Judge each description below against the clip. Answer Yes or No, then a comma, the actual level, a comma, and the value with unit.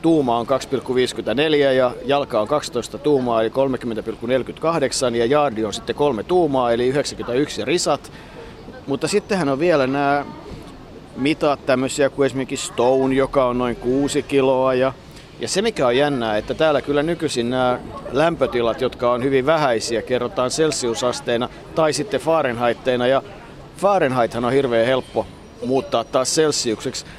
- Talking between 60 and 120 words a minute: No, average, 140 wpm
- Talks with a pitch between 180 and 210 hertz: No, low, 130 Hz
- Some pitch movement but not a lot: Yes, average, 3.0 semitones